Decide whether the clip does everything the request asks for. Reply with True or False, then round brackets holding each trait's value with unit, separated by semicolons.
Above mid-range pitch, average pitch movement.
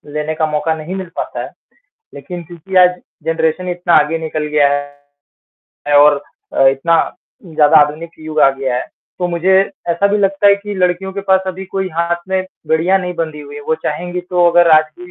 False (170 Hz; 3.1 semitones)